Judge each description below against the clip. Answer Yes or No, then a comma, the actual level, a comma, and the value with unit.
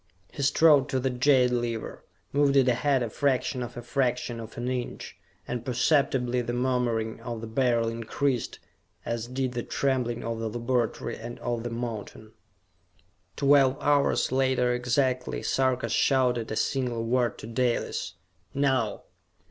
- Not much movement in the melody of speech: Yes, narrow, 2.1 semitones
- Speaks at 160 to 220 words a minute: No, average, 150 wpm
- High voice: No, low, 125 Hz